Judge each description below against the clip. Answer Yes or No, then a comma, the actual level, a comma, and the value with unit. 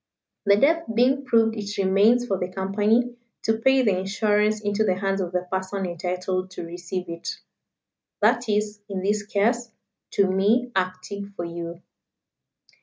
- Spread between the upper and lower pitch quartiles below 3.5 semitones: Yes, average, 3.1 semitones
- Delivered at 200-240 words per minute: No, average, 155 wpm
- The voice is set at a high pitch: Yes, high, 200 Hz